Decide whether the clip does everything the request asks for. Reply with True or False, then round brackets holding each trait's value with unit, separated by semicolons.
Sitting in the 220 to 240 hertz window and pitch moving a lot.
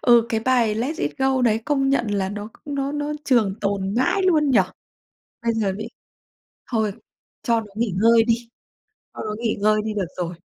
False (230 Hz; 3.9 semitones)